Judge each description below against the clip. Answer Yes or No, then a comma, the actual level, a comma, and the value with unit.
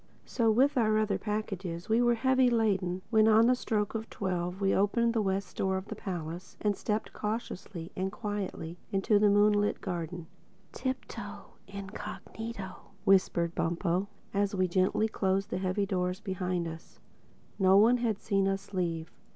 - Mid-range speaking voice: No, high, 195 Hz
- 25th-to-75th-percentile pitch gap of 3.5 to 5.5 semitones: No, average, 2.8 semitones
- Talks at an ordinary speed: Yes, average, 160 wpm